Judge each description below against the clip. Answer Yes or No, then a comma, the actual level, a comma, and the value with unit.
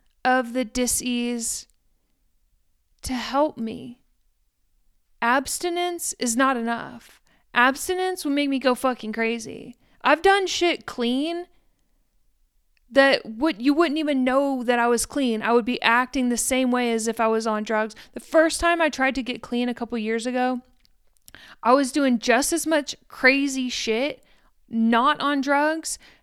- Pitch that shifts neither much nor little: Yes, average, 3.5 semitones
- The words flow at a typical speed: Yes, average, 155 wpm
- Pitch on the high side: Yes, very high, 255 Hz